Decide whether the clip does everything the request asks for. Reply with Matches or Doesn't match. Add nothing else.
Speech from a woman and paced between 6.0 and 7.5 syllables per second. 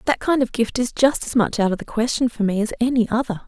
Matches